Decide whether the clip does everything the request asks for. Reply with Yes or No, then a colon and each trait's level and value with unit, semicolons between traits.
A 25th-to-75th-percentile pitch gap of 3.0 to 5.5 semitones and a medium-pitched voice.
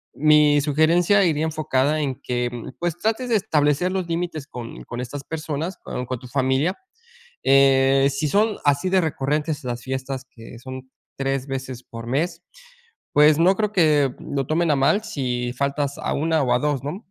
Yes: average, 3.8 semitones; medium, 145 Hz